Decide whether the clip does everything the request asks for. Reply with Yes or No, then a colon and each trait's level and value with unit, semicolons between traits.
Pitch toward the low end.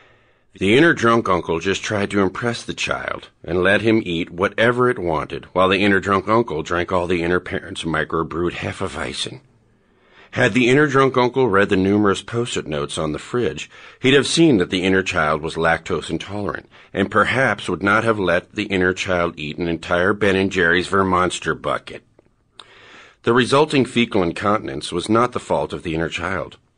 Yes: very low, 95 Hz